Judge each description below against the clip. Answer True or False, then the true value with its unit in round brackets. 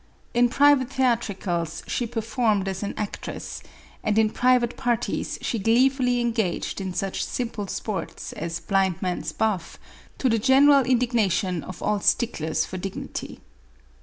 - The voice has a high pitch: True (220 Hz)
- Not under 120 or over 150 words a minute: True (140 wpm)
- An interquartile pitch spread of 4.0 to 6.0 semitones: True (4.3 semitones)